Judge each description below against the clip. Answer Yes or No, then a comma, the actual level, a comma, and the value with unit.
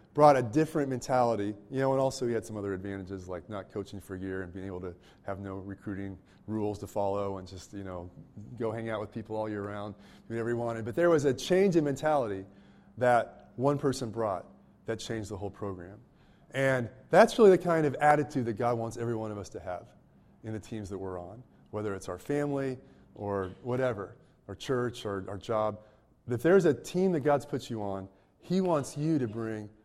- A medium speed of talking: No, fast, 220 wpm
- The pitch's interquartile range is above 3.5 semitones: Yes, average, 5.2 semitones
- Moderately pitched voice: No, low, 110 Hz